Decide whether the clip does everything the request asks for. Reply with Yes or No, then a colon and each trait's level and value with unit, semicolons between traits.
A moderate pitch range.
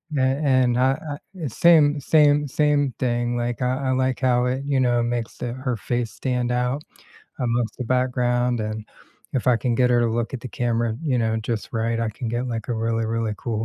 No: narrow, 1.9 semitones